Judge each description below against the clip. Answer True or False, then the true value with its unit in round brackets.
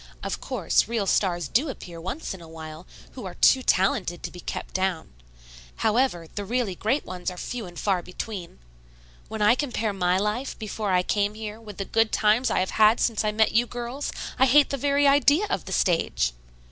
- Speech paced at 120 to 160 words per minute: False (205 wpm)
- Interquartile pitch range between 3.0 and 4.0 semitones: False (4.9 semitones)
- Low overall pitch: False (210 Hz)